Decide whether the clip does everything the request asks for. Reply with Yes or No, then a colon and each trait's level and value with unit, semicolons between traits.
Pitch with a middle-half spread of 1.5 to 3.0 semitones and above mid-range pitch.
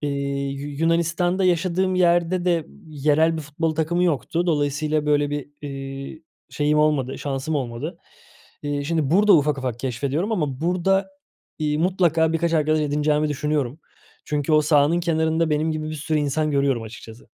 No: narrow, 2.6 semitones; medium, 155 Hz